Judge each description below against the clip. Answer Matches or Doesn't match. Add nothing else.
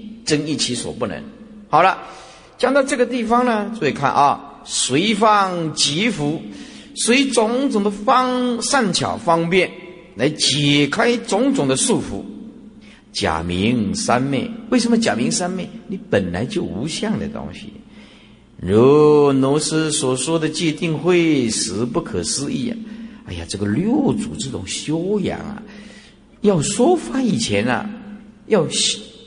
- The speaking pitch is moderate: Doesn't match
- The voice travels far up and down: Matches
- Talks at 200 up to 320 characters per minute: Doesn't match